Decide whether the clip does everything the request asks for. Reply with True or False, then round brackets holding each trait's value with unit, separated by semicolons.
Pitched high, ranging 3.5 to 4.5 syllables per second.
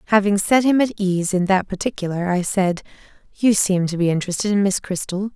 False (195 Hz; 5.7 syllables/s)